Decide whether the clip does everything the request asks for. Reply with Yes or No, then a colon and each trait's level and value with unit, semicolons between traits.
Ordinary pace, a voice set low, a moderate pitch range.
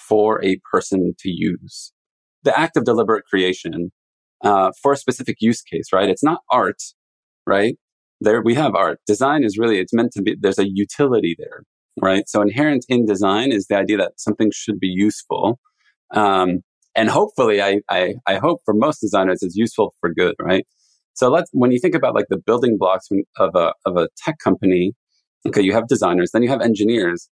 Yes: average, 195 wpm; low, 105 Hz; average, 3.7 semitones